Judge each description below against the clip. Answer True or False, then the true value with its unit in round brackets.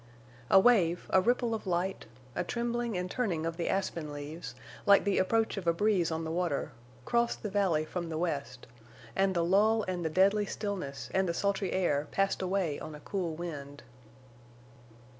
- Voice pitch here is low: False (180 Hz)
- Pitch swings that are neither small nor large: True (3.6 semitones)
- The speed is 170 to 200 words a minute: True (180 wpm)